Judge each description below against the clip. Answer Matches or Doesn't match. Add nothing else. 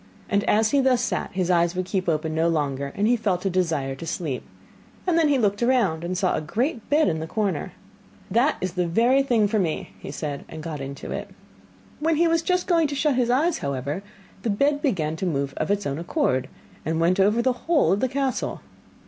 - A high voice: Matches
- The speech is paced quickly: Matches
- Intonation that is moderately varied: Doesn't match